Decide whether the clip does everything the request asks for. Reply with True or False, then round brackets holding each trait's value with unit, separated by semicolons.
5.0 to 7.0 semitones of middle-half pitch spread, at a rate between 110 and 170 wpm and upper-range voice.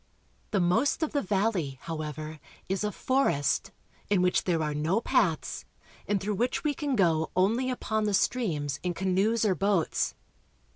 True (5.5 semitones; 160 wpm; 195 Hz)